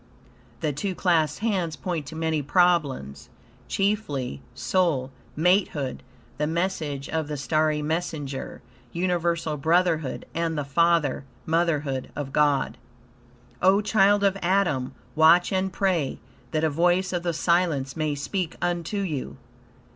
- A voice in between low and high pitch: Yes, medium, 160 Hz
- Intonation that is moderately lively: Yes, average, 3.5 semitones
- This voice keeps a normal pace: No, slow, 125 wpm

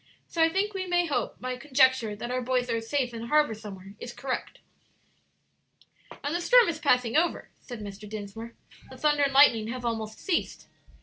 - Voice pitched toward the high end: Yes, very high, 250 Hz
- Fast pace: No, average, 185 wpm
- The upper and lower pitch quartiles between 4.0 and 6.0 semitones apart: Yes, average, 4.9 semitones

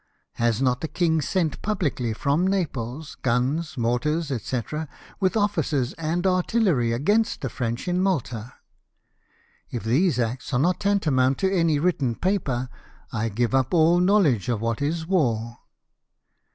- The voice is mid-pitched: Yes, medium, 145 Hz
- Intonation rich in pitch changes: Yes, wide, 6.7 semitones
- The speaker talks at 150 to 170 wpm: No, average, 140 wpm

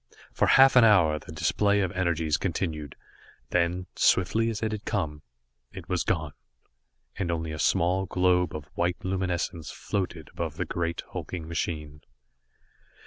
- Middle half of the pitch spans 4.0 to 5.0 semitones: No, average, 3.0 semitones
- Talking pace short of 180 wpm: Yes, average, 145 wpm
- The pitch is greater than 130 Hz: No, very low, 85 Hz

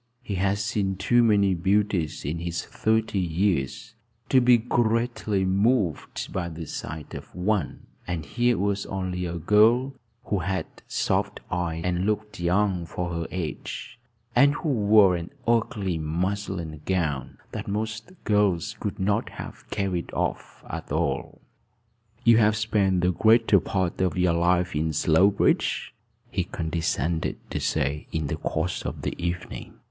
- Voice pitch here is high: No, very low, 95 Hz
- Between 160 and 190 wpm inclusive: No, average, 145 wpm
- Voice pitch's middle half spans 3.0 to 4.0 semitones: Yes, average, 3.7 semitones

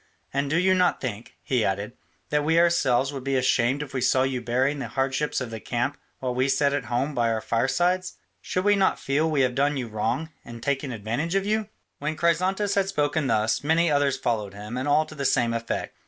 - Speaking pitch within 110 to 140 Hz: Yes, low, 135 Hz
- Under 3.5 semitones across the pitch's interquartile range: No, average, 4.5 semitones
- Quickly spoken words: Yes, fast, 230 wpm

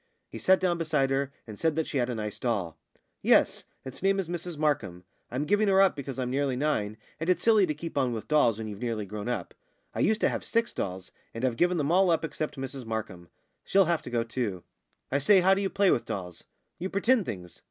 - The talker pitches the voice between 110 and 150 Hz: Yes, medium, 140 Hz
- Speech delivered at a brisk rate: Yes, fast, 240 wpm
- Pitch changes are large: Yes, wide, 7.7 semitones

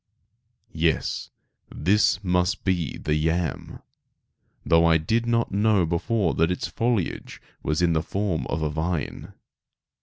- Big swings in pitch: No, average, 4.0 semitones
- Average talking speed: No, slow, 130 wpm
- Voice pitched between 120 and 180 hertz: No, very low, 90 Hz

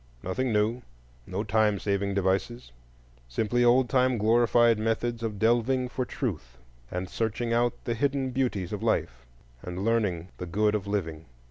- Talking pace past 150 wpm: No, average, 145 wpm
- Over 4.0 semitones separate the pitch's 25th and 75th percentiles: Yes, average, 4.4 semitones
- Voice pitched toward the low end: Yes, low, 110 Hz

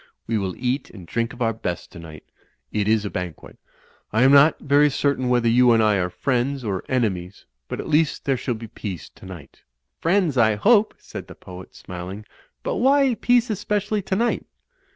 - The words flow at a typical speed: Yes, average, 190 wpm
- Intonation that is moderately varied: No, wide, 6.9 semitones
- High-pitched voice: No, low, 120 Hz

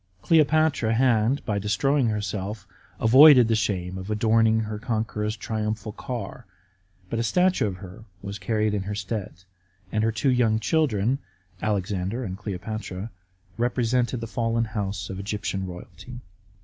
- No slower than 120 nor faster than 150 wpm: Yes, average, 140 wpm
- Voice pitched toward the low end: Yes, low, 110 Hz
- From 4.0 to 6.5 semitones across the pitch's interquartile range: No, average, 2.8 semitones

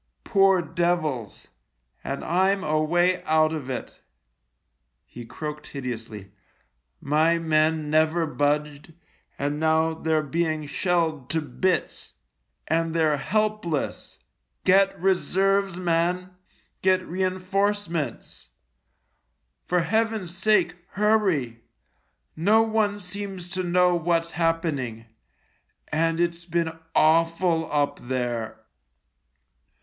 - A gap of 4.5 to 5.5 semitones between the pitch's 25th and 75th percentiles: No, average, 3.4 semitones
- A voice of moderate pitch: Yes, medium, 165 Hz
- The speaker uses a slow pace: Yes, slow, 100 wpm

